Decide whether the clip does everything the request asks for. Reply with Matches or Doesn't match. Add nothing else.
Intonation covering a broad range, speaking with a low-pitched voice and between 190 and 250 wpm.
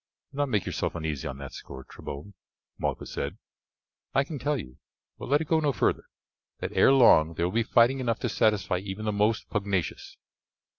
Matches